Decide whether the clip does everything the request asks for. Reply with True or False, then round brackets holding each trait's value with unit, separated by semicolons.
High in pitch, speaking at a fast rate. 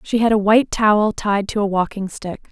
True (205 Hz; 240 wpm)